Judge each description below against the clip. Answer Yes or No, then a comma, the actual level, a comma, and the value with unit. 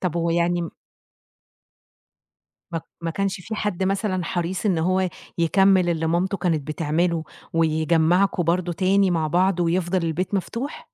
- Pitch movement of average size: No, narrow, 2.2 semitones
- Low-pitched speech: No, medium, 175 Hz